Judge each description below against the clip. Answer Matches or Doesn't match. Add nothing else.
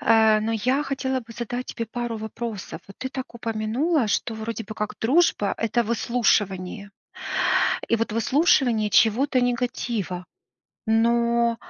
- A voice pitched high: Matches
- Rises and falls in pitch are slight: Matches